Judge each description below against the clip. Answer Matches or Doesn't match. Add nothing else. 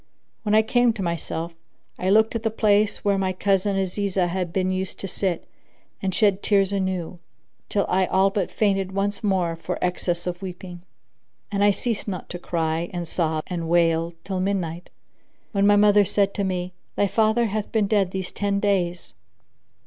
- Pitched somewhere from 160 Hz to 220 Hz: Matches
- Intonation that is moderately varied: Doesn't match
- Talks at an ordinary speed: Matches